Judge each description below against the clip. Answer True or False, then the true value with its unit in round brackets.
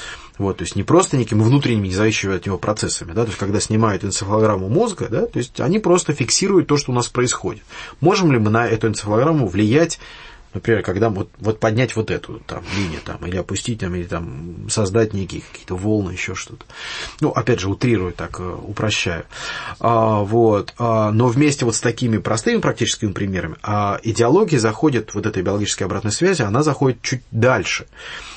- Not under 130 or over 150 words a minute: False (185 wpm)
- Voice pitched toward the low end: True (110 Hz)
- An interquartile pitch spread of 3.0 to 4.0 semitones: True (3.6 semitones)